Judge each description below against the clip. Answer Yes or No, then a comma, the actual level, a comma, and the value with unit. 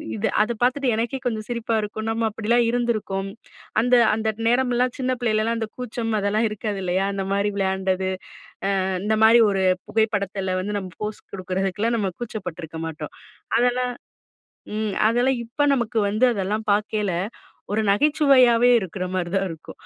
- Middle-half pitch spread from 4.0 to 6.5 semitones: No, average, 3.5 semitones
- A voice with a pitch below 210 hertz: No, high, 215 Hz